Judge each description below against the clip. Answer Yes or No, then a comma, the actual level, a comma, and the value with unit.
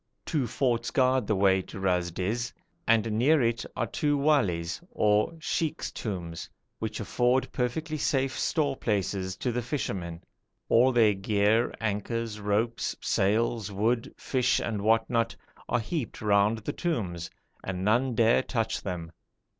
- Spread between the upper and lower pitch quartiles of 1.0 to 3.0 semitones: No, average, 3.7 semitones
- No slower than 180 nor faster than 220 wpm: No, average, 145 wpm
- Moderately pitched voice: No, low, 115 Hz